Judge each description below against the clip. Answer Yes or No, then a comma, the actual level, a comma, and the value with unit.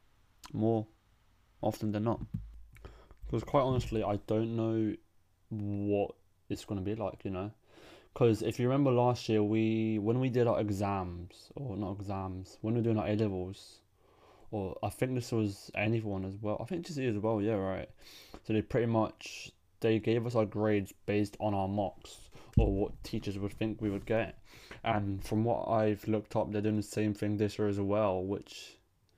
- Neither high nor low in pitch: No, low, 105 Hz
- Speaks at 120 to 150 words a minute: No, average, 190 wpm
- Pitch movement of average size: No, narrow, 1.9 semitones